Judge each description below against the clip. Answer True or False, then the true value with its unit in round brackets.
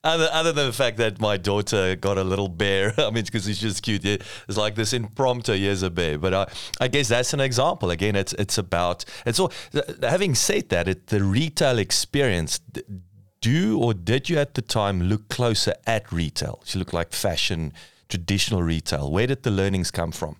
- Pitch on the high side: False (105 Hz)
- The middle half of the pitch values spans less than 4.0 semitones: False (4.4 semitones)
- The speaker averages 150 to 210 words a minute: True (200 wpm)